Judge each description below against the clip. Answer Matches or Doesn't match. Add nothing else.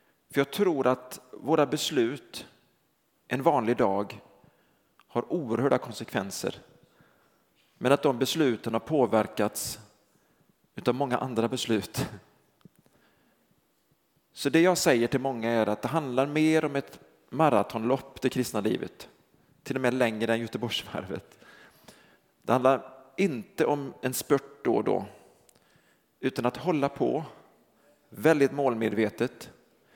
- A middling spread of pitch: Matches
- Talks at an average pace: Doesn't match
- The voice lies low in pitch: Matches